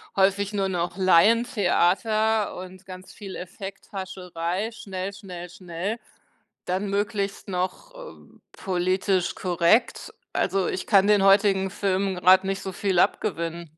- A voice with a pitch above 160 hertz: Yes, high, 190 Hz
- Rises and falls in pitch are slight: Yes, narrow, 1.8 semitones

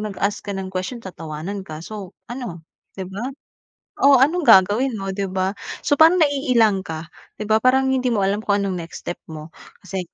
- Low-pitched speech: No, high, 200 Hz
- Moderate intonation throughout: Yes, average, 4.7 semitones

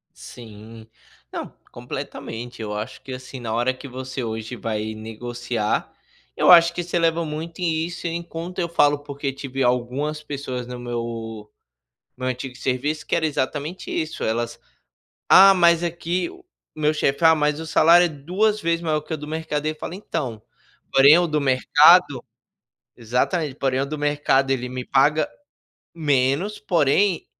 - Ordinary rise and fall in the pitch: Yes, average, 4.8 semitones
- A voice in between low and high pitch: Yes, medium, 145 Hz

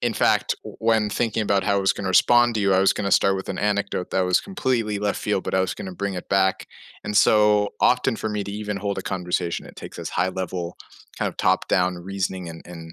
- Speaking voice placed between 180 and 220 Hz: No, low, 100 Hz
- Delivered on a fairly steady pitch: Yes, narrow, 2.1 semitones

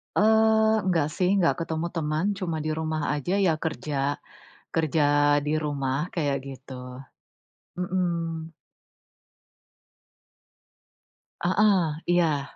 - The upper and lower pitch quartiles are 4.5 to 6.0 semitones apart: No, average, 3.1 semitones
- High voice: No, medium, 160 Hz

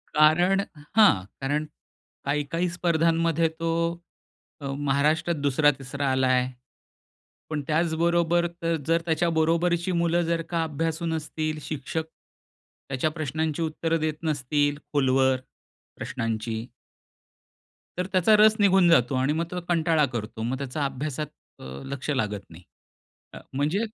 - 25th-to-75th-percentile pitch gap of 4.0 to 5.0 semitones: No, average, 3.4 semitones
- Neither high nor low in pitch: Yes, medium, 155 Hz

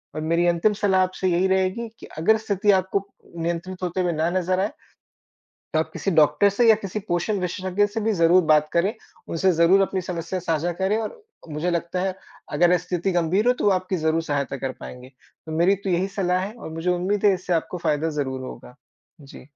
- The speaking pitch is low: No, medium, 180 Hz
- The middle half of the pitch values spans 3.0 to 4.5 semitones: No, narrow, 2.6 semitones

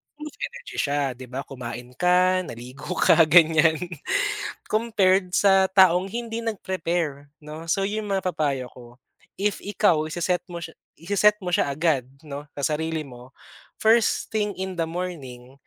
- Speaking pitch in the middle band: Yes, medium, 170 Hz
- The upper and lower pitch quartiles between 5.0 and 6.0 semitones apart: Yes, average, 5.3 semitones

